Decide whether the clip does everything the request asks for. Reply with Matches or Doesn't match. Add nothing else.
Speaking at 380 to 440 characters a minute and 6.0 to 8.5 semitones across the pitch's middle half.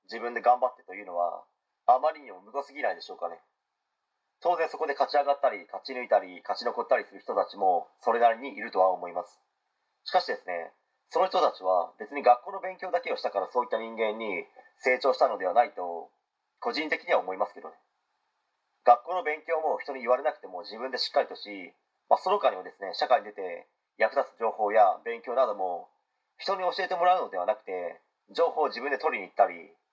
Matches